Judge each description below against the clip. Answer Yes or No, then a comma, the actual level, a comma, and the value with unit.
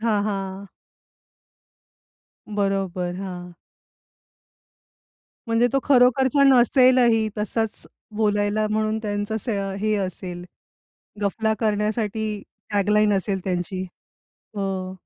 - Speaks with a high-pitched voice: Yes, high, 210 Hz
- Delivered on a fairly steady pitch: Yes, narrow, 2.3 semitones